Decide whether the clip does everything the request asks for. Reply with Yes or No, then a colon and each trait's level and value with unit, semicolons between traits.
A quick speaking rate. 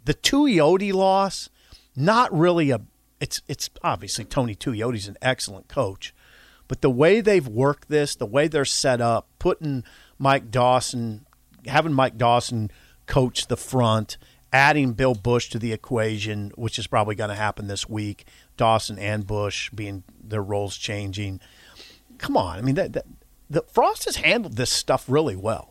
No: average, 160 wpm